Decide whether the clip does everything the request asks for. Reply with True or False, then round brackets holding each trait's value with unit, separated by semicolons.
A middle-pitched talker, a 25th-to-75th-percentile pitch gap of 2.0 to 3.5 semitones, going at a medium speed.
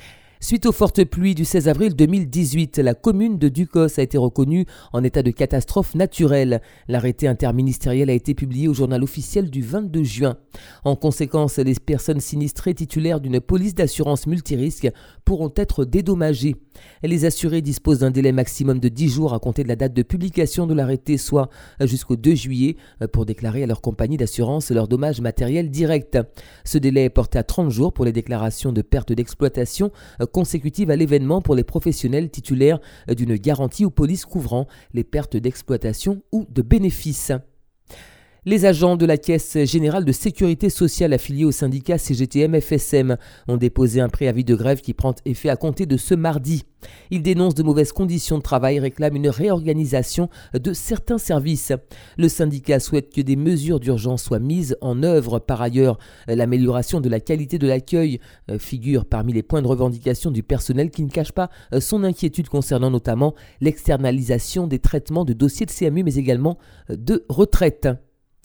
False (145 Hz; 4.2 semitones; 170 wpm)